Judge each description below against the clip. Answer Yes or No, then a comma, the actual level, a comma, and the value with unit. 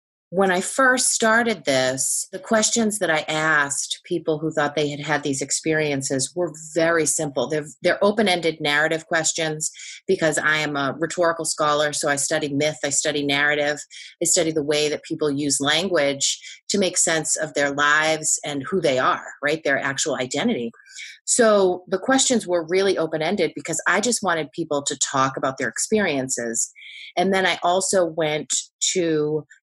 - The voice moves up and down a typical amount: Yes, average, 3.5 semitones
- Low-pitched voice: No, medium, 155 Hz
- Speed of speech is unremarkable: Yes, average, 170 wpm